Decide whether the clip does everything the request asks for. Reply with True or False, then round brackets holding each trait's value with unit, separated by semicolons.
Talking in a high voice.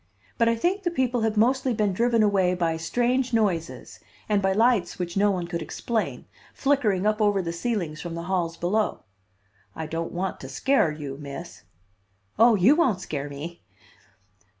True (195 Hz)